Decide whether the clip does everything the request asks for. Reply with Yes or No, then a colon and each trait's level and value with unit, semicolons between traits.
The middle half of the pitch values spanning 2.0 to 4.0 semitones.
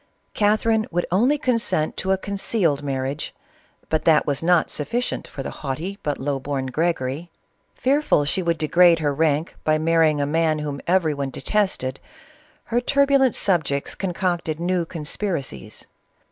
No: average, 4.8 semitones